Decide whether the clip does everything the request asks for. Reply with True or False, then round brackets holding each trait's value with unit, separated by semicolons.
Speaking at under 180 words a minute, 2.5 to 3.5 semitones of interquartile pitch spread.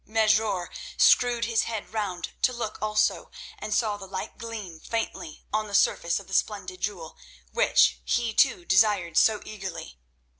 True (155 wpm; 3.0 semitones)